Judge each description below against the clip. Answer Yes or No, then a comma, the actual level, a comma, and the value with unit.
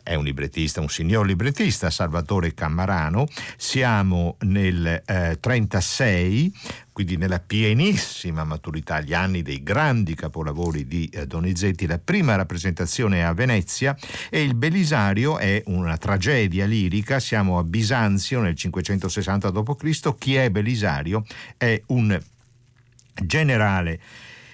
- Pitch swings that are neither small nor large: No, wide, 5.7 semitones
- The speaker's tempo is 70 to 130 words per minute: Yes, average, 120 wpm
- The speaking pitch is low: Yes, low, 100 Hz